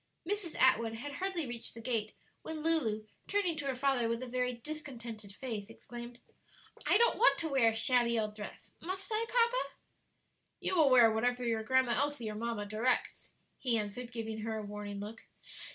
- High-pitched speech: Yes, high, 240 Hz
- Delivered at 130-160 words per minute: No, average, 185 wpm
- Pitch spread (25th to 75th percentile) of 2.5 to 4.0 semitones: No, average, 4.5 semitones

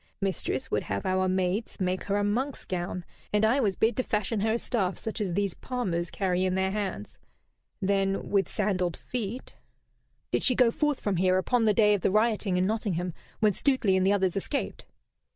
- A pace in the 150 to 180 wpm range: No, fast, 205 wpm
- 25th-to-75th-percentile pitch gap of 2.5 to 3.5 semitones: Yes, average, 2.9 semitones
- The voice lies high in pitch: Yes, high, 200 Hz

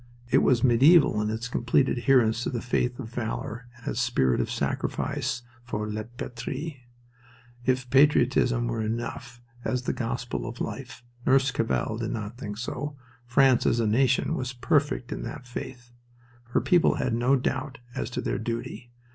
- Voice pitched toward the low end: Yes, low, 120 Hz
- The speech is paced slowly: No, average, 165 wpm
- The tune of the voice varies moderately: No, narrow, 2.1 semitones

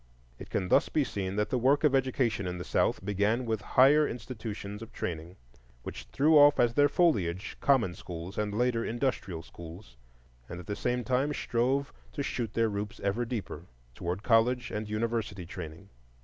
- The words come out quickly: No, average, 175 wpm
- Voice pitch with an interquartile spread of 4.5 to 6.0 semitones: Yes, average, 4.9 semitones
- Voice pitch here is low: Yes, low, 110 Hz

